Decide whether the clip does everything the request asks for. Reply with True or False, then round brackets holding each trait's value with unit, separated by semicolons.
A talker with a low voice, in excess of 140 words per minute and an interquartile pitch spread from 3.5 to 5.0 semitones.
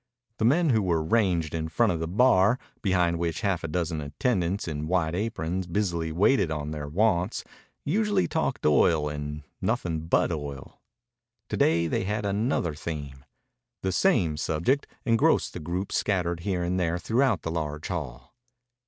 True (85 Hz; 160 wpm; 4.7 semitones)